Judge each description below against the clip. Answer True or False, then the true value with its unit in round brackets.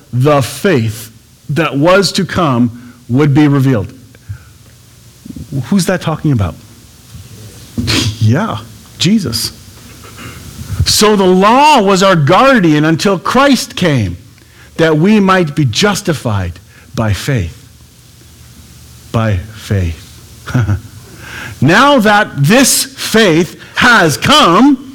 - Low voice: True (125 Hz)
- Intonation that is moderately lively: False (8.2 semitones)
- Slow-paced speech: True (95 wpm)